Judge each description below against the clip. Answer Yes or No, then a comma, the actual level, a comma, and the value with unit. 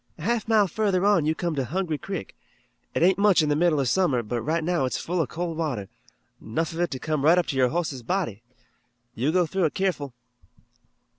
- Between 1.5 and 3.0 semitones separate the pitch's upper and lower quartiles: No, average, 4.6 semitones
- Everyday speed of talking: No, fast, 225 wpm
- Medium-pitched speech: Yes, medium, 165 Hz